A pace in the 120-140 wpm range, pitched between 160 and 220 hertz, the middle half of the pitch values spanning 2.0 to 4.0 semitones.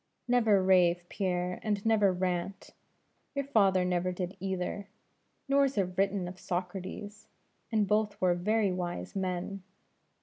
Yes: slow, 135 wpm; high, 190 Hz; narrow, 2.4 semitones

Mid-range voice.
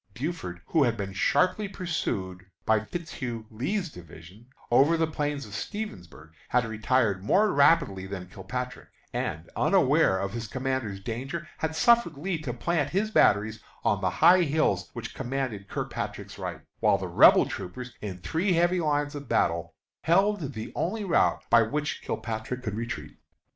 No: low, 125 Hz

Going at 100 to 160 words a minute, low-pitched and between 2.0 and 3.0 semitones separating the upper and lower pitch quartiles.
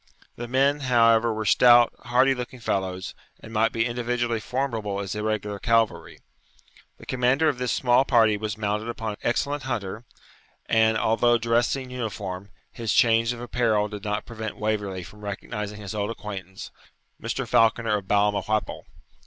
Yes: average, 155 wpm; low, 115 Hz; narrow, 2.5 semitones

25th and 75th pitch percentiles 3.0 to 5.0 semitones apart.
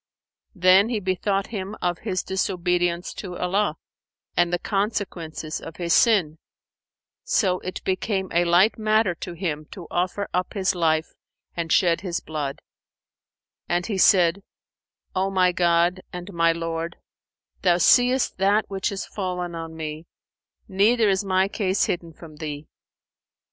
No: narrow, 2.4 semitones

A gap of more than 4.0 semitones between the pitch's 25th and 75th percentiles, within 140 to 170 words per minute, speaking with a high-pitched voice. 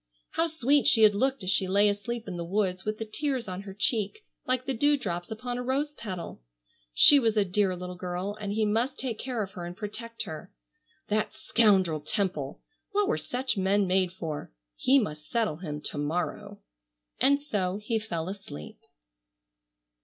No: average, 4.7 semitones; average, 185 wpm; high, 205 Hz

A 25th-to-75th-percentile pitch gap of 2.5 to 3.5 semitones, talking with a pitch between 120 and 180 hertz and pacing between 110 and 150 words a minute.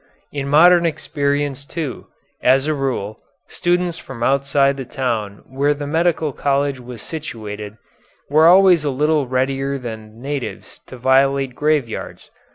Yes: average, 2.8 semitones; medium, 140 Hz; average, 140 wpm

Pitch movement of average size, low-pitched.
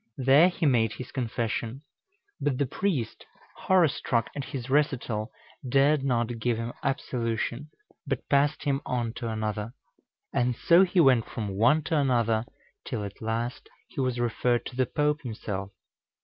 Yes: average, 3.7 semitones; low, 125 Hz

